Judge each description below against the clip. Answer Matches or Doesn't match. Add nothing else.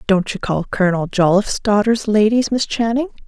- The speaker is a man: Doesn't match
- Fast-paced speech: Doesn't match